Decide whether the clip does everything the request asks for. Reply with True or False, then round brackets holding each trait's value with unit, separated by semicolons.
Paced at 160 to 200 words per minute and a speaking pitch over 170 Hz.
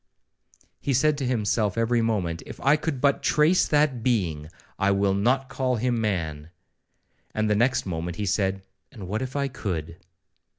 False (165 wpm; 110 Hz)